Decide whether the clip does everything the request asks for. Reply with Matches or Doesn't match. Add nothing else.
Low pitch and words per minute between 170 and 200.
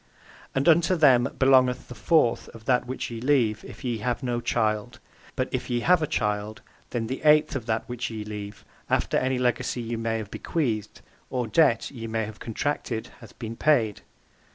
Matches